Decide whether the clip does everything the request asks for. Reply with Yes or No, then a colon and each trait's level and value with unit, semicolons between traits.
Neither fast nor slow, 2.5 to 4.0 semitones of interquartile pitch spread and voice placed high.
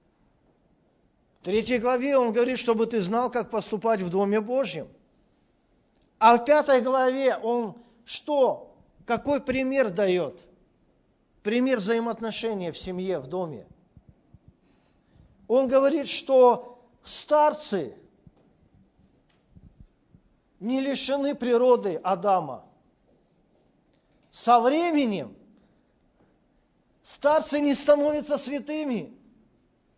No: slow, 85 wpm; average, 3.5 semitones; high, 245 Hz